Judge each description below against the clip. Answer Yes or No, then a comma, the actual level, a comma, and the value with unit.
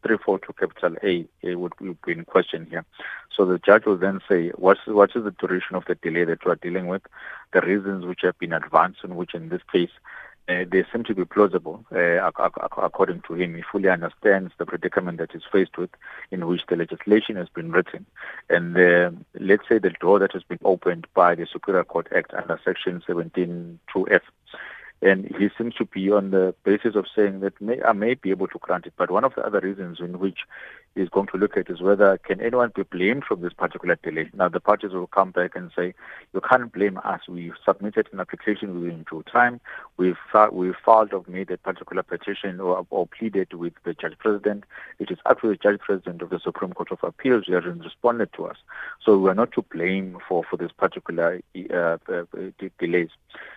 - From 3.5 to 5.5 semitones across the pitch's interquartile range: No, narrow, 2.4 semitones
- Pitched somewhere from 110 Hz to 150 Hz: No, very low, 95 Hz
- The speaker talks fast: Yes, fast, 215 wpm